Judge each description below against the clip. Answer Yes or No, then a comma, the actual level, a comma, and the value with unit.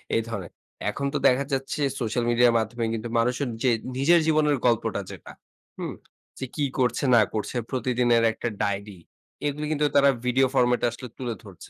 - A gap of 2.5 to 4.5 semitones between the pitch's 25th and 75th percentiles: Yes, average, 2.9 semitones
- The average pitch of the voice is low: Yes, low, 125 Hz